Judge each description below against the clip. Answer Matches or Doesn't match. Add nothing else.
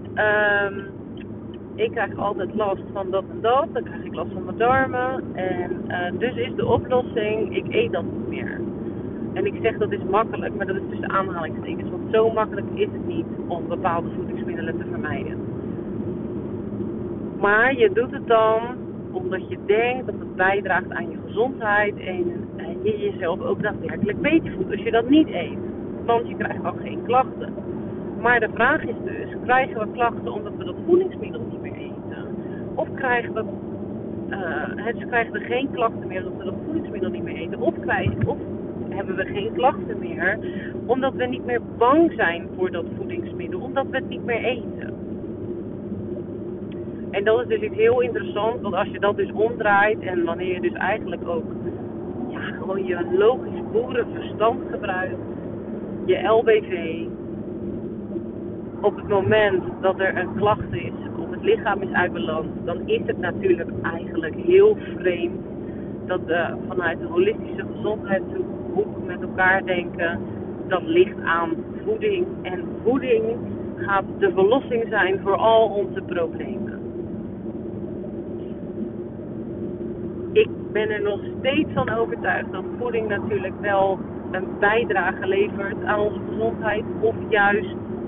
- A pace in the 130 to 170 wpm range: Matches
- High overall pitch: Matches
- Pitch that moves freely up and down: Matches